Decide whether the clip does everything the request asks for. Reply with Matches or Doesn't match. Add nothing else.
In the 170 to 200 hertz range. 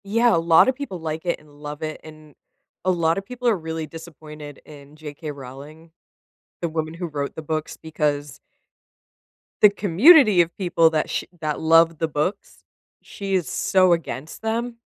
Doesn't match